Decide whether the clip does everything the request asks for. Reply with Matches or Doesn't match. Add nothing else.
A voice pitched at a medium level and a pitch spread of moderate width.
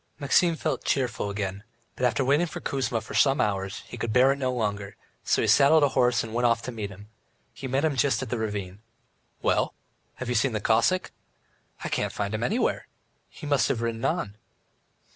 Doesn't match